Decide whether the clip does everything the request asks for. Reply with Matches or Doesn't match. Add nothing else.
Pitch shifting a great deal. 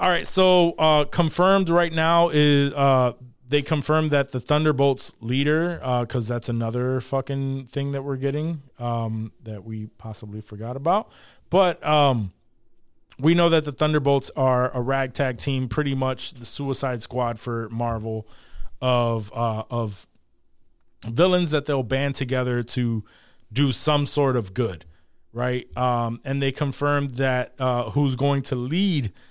Doesn't match